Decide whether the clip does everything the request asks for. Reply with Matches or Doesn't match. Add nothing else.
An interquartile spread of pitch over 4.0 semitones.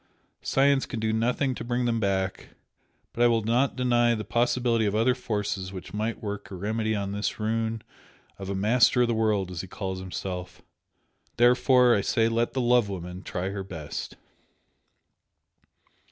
Doesn't match